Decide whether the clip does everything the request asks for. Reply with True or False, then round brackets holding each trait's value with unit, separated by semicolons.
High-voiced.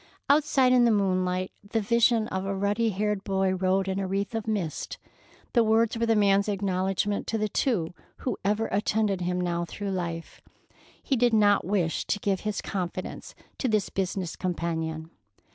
True (200 Hz)